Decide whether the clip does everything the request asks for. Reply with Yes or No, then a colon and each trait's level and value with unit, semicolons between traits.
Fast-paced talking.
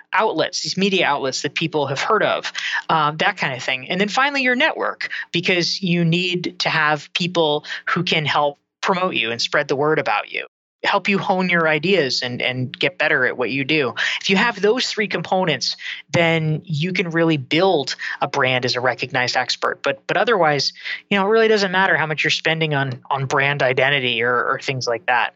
Yes: fast, 210 wpm